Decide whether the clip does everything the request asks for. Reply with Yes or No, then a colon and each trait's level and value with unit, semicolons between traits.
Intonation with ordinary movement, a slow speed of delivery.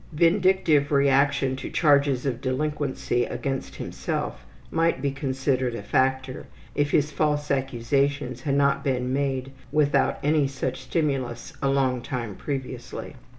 No: narrow, 2.0 semitones; slow, 130 wpm